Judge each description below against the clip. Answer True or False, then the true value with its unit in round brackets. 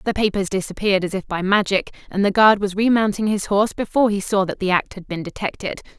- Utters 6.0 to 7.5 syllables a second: True (6.4 syllables/s)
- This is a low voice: False (200 Hz)